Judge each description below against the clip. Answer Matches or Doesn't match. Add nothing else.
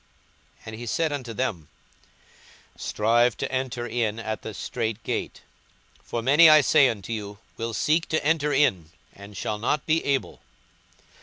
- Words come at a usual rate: Matches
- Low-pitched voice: Matches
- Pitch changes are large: Doesn't match